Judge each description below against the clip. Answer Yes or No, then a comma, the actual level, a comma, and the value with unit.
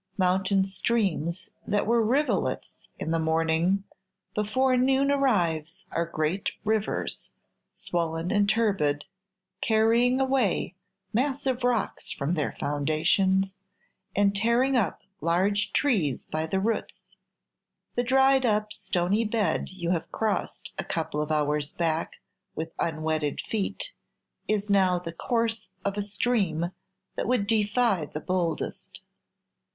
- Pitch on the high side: Yes, high, 195 Hz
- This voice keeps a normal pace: No, slow, 120 wpm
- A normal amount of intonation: No, wide, 5.7 semitones